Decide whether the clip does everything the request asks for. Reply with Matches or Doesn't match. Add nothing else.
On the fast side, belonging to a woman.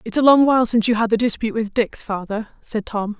Matches